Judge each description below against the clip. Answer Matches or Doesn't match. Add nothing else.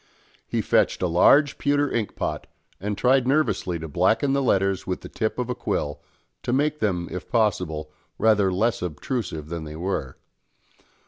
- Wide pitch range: Matches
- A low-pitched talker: Matches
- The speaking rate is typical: Matches